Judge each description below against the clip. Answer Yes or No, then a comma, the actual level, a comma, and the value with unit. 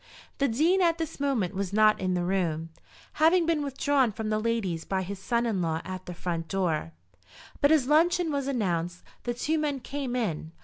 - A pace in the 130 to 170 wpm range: No, average, 195 wpm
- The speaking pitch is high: Yes, high, 225 Hz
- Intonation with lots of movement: Yes, wide, 7.9 semitones